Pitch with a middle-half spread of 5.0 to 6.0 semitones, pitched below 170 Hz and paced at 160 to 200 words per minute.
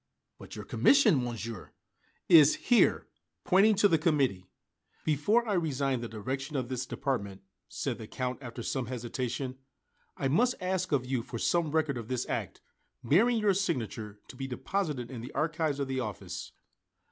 Yes: average, 5.3 semitones; low, 135 Hz; average, 165 wpm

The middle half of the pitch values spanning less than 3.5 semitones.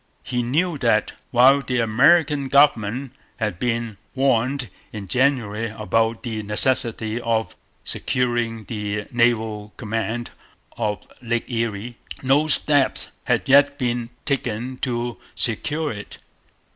Yes: average, 3.1 semitones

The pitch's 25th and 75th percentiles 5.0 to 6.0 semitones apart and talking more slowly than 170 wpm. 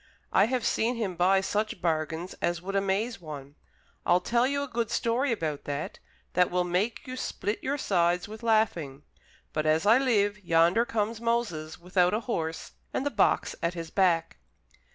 No: average, 5.3 semitones; average, 175 wpm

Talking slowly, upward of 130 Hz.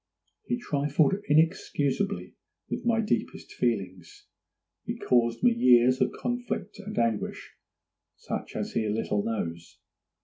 Yes: slow, 115 wpm; medium, 140 Hz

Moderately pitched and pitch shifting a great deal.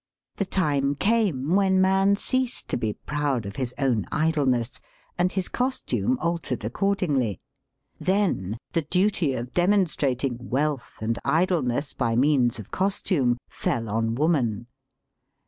Yes: medium, 145 Hz; wide, 7.5 semitones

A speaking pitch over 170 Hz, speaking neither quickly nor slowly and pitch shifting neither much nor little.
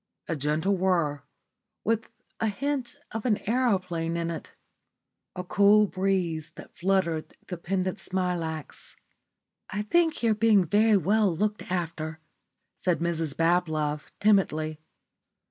No: medium, 185 Hz; slow, 120 wpm; average, 4.2 semitones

